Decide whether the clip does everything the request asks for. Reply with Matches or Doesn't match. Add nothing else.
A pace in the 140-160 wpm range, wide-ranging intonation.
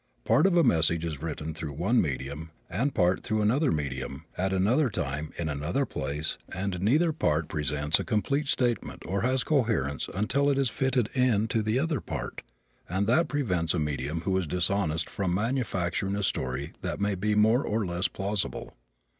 Doesn't match